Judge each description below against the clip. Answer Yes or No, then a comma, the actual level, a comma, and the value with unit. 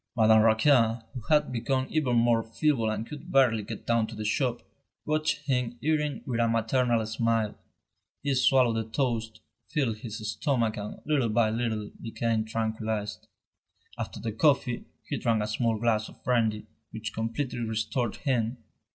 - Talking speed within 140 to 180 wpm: Yes, average, 160 wpm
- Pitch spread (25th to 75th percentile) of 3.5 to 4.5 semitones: No, narrow, 2.6 semitones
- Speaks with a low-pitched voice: Yes, low, 115 Hz